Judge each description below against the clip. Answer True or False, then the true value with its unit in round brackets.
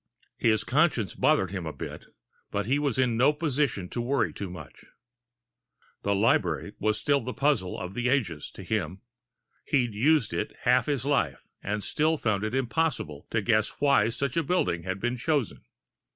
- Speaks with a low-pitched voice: True (120 Hz)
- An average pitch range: False (5.8 semitones)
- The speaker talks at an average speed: True (175 wpm)